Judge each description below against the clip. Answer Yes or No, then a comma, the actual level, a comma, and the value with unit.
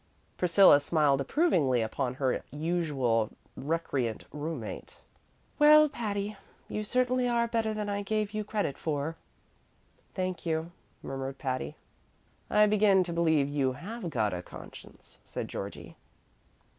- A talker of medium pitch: Yes, medium, 170 Hz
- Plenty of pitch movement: Yes, wide, 7.5 semitones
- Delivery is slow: Yes, slow, 130 wpm